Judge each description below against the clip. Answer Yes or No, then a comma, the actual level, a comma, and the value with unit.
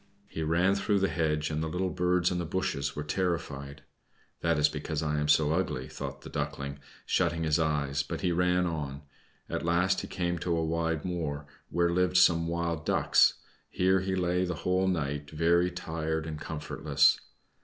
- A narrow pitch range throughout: No, average, 3.0 semitones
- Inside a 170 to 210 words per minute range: Yes, average, 185 wpm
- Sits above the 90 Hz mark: No, very low, 85 Hz